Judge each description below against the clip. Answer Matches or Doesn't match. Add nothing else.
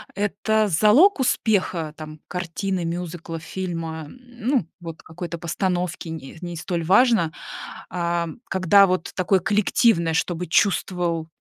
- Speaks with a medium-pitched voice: Matches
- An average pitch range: Matches